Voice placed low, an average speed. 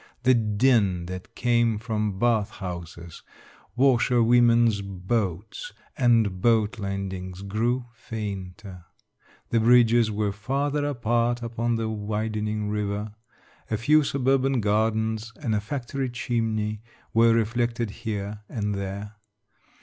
No: low, 110 Hz; slow, 110 wpm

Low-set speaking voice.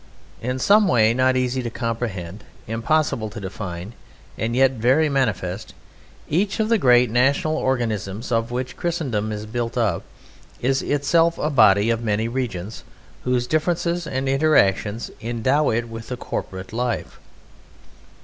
Yes: low, 120 Hz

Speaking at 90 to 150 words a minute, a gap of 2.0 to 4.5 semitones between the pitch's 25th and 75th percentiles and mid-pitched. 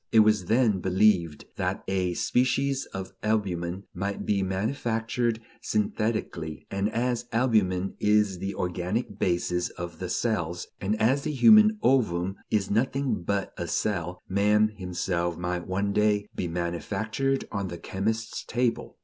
No: average, 140 wpm; average, 3.8 semitones; low, 100 Hz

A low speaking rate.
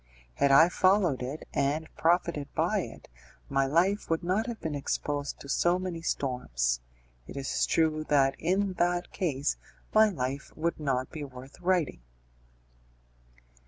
No: average, 145 wpm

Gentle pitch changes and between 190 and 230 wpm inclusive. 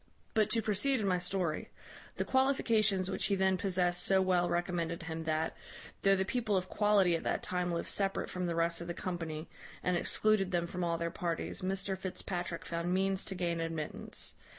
Yes: narrow, 2.3 semitones; average, 195 wpm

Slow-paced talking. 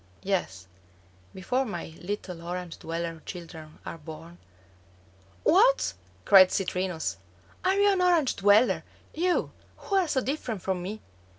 Yes: slow, 130 wpm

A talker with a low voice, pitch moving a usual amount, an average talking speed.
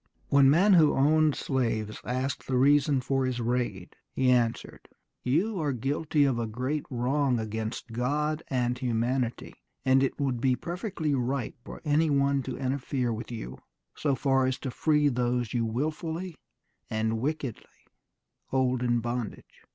Yes: low, 130 Hz; average, 3.2 semitones; average, 150 wpm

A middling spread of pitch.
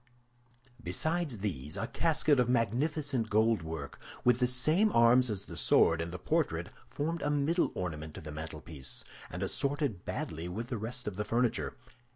No: wide, 8.3 semitones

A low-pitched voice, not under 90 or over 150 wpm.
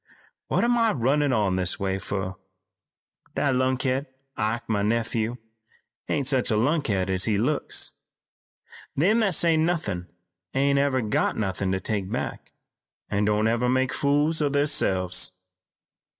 Yes: low, 120 Hz; average, 140 wpm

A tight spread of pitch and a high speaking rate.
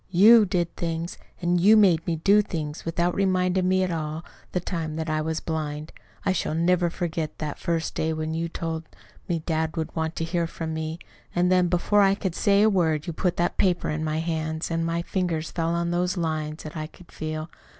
Yes: narrow, 2.2 semitones; fast, 210 wpm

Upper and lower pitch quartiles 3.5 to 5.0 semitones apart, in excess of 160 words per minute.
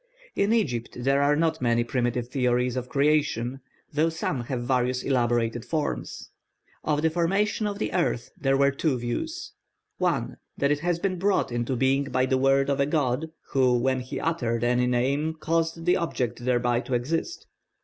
Yes: average, 4.6 semitones; average, 175 wpm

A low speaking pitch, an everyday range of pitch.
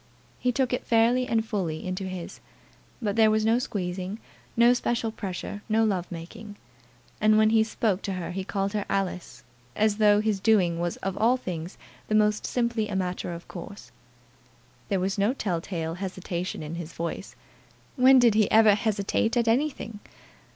No: high, 205 Hz; average, 3.5 semitones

